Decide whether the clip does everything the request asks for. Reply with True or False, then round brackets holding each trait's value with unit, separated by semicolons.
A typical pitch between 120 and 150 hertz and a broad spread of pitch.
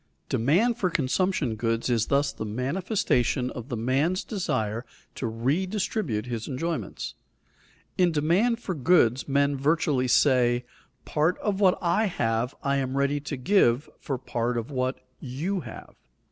True (140 Hz; 6.1 semitones)